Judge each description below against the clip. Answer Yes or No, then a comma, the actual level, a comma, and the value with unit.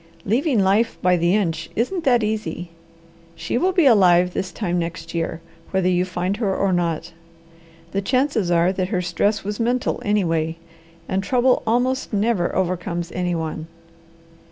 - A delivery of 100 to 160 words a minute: Yes, average, 155 wpm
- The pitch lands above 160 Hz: Yes, high, 190 Hz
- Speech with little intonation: No, average, 4.2 semitones